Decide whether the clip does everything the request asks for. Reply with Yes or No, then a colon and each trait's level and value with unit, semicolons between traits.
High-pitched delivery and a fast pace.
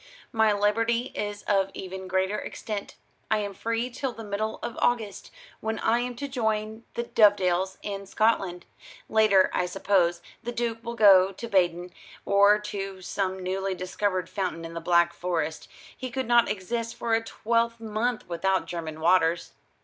No: high, 205 Hz; average, 160 wpm